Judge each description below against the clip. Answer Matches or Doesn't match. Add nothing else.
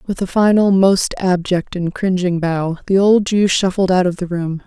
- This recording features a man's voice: Doesn't match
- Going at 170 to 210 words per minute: Matches